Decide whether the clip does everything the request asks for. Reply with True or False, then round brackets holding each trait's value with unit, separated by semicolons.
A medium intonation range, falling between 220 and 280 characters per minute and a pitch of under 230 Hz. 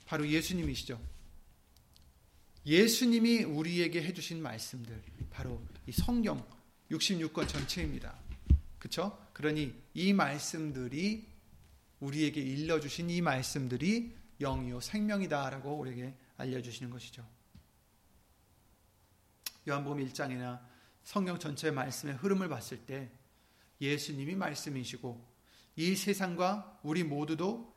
False (6.6 semitones; 255 characters per minute; 140 Hz)